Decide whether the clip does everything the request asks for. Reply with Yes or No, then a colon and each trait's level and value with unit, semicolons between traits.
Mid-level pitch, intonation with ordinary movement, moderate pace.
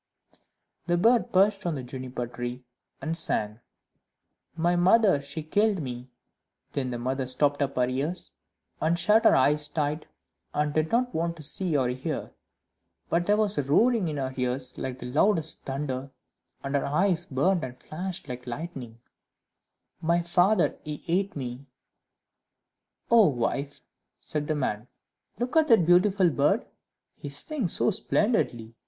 No: medium, 150 Hz; wide, 5.7 semitones; average, 150 wpm